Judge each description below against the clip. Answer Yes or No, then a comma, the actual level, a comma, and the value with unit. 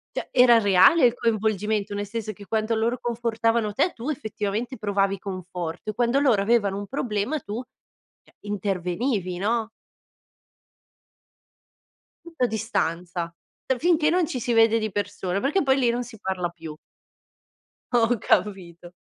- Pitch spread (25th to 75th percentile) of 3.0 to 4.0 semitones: Yes, average, 3.4 semitones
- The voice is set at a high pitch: Yes, high, 220 Hz